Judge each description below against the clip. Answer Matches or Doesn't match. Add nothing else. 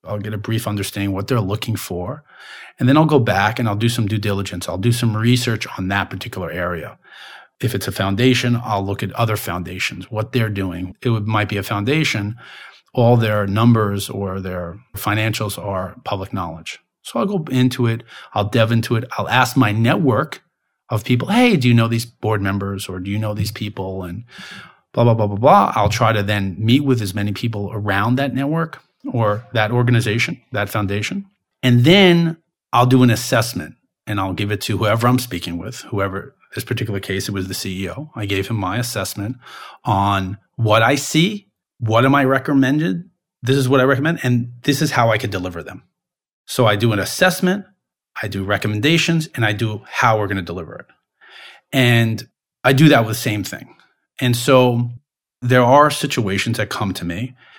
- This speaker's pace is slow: Doesn't match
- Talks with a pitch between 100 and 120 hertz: Matches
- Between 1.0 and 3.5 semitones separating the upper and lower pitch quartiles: Doesn't match